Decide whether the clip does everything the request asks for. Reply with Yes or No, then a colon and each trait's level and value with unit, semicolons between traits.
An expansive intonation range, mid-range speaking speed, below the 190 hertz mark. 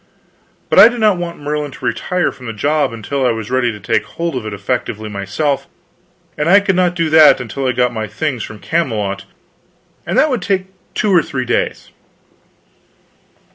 Yes: wide, 7.2 semitones; average, 190 wpm; medium, 140 Hz